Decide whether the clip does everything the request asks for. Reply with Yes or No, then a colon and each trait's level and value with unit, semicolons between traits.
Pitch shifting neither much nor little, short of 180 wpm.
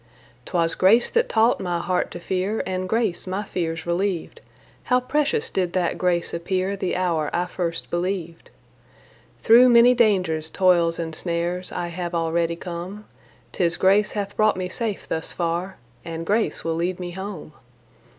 Yes: average, 3.0 semitones; average, 160 wpm